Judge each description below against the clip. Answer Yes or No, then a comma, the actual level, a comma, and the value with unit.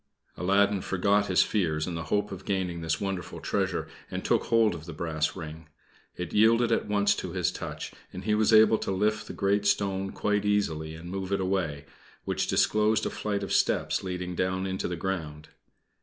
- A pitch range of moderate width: Yes, average, 3.2 semitones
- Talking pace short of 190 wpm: No, average, 195 wpm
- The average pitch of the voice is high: No, very low, 95 Hz